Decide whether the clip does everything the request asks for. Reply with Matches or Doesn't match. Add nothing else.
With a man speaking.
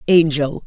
Doesn't match